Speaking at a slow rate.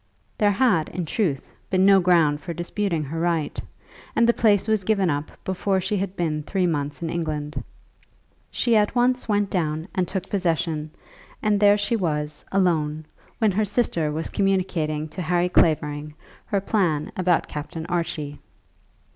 No: average, 165 wpm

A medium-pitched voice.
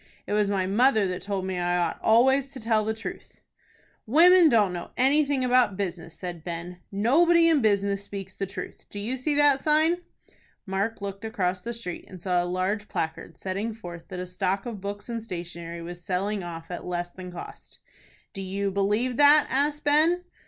No: high, 200 Hz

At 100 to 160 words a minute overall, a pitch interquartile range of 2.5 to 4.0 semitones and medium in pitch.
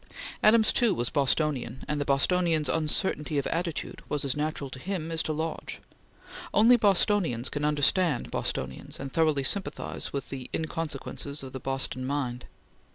Yes: average, 155 wpm; average, 3.4 semitones; medium, 150 Hz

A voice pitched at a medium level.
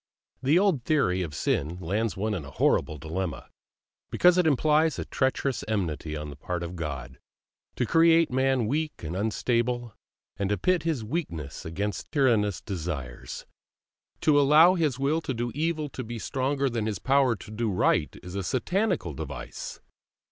No: low, 115 Hz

